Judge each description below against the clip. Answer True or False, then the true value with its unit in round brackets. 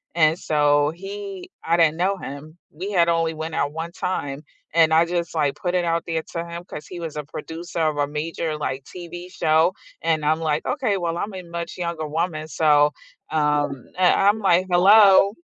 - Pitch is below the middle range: False (165 Hz)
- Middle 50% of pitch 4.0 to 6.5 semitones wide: False (2.5 semitones)